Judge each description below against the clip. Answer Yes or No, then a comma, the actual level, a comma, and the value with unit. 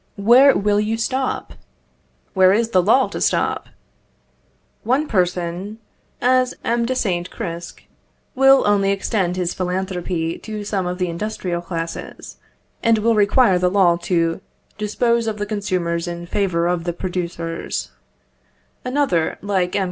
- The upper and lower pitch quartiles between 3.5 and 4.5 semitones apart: Yes, average, 4.0 semitones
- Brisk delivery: No, average, 140 wpm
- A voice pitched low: No, high, 190 Hz